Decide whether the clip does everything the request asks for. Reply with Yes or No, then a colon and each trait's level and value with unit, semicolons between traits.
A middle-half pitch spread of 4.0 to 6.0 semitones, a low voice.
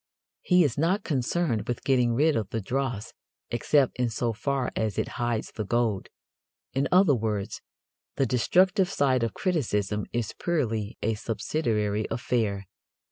Yes: average, 4.6 semitones; low, 120 Hz